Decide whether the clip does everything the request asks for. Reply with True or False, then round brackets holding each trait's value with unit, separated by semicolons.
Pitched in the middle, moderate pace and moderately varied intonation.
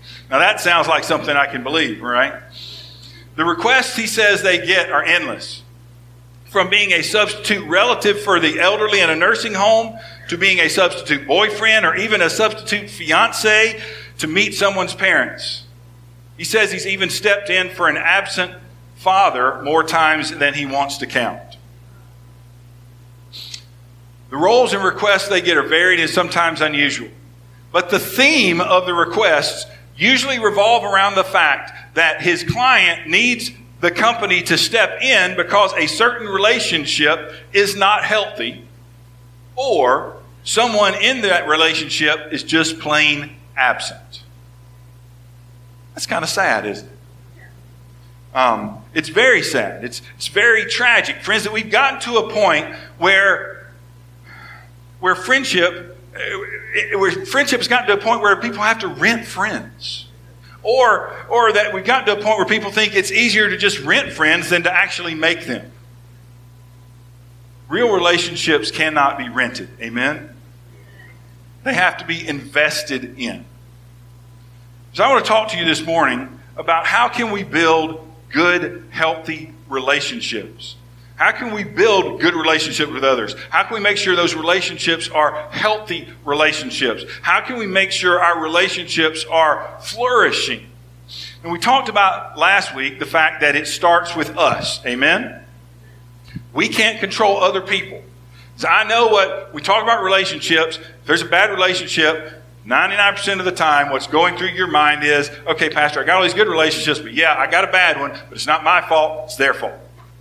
False (160 Hz; 160 wpm; 8.0 semitones)